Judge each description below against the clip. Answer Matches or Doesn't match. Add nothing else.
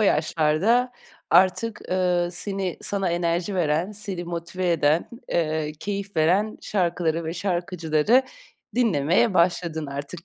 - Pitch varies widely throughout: Doesn't match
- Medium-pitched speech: Matches